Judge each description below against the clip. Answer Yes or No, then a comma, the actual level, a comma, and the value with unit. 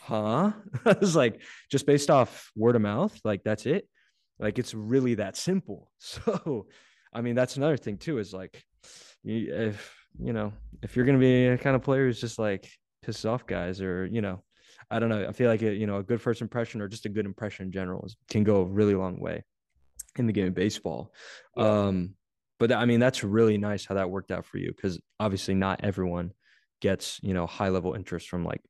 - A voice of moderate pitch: No, low, 105 Hz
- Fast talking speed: Yes, fast, 215 wpm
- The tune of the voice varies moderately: Yes, average, 3.8 semitones